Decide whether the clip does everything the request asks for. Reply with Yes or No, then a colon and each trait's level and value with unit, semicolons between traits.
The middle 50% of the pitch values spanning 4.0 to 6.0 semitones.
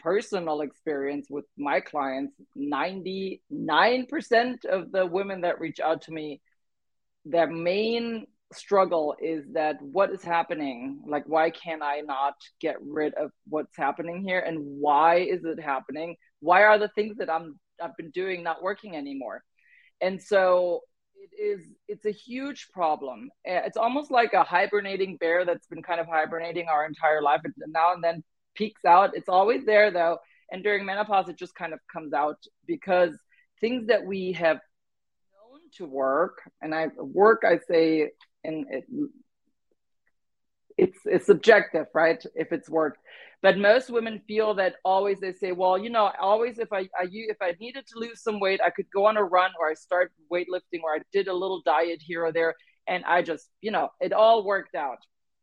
Yes: average, 4.9 semitones